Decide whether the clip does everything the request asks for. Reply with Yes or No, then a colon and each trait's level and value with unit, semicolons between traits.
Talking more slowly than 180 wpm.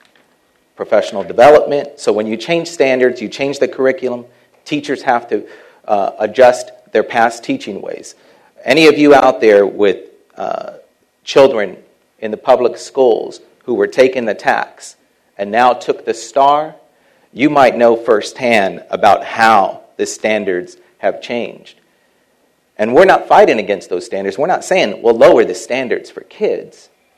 Yes: average, 150 wpm